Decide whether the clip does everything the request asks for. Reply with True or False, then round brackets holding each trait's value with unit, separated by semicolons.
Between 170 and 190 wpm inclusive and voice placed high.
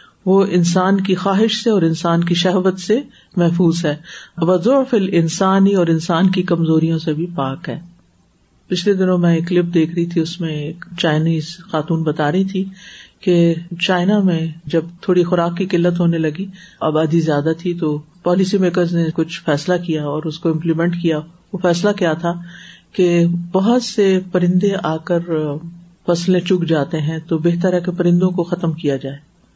False (175 wpm; 175 Hz)